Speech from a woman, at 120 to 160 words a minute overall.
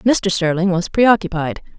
Yes: female; slow, 135 wpm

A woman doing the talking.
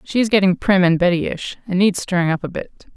Yes: female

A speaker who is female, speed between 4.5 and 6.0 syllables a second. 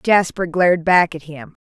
Yes: female; 4.6 syllables/s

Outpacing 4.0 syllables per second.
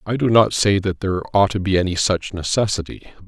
Yes: 5.7 syllables/s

